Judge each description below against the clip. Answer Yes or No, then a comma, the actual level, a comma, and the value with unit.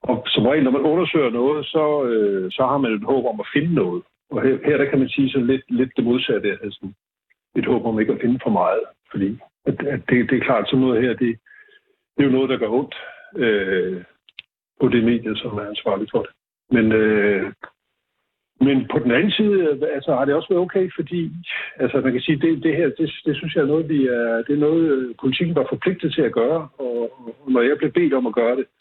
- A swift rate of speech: Yes, fast, 235 wpm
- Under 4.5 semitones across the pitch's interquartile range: No, wide, 5.4 semitones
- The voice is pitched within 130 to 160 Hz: Yes, low, 135 Hz